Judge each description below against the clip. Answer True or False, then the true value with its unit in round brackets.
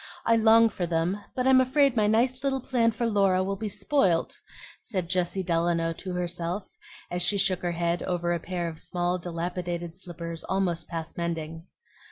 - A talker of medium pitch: True (180 Hz)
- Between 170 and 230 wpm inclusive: True (180 wpm)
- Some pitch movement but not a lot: True (3.7 semitones)